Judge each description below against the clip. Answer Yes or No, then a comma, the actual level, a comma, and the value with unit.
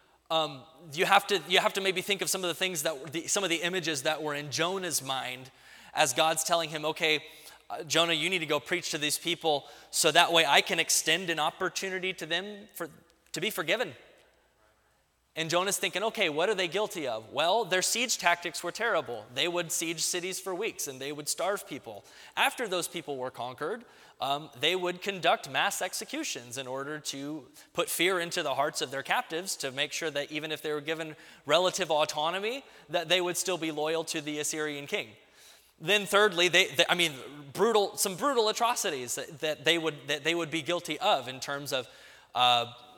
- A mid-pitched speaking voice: Yes, medium, 165 Hz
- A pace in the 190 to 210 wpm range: Yes, fast, 205 wpm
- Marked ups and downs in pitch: No, average, 3.5 semitones